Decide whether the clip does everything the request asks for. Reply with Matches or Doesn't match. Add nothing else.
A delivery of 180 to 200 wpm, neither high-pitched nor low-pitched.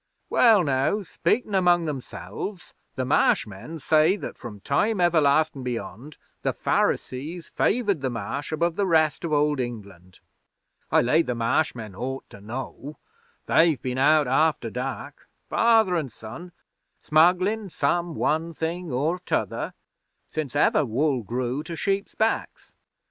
Doesn't match